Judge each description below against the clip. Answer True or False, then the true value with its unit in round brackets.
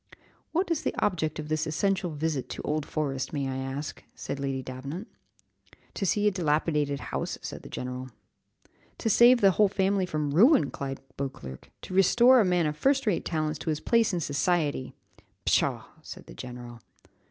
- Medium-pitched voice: True (155 Hz)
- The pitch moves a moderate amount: False (5.9 semitones)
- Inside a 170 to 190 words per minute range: True (175 wpm)